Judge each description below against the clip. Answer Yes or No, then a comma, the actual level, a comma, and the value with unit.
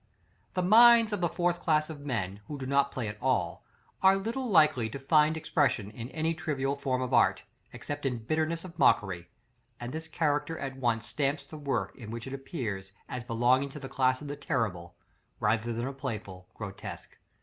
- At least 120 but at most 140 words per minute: No, average, 195 wpm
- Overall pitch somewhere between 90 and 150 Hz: Yes, low, 135 Hz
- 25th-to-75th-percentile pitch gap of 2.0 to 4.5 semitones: No, average, 5.1 semitones